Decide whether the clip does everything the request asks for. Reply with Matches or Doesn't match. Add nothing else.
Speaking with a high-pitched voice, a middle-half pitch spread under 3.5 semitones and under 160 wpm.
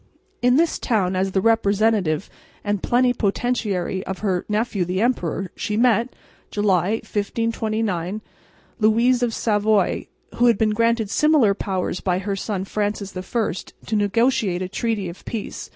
Matches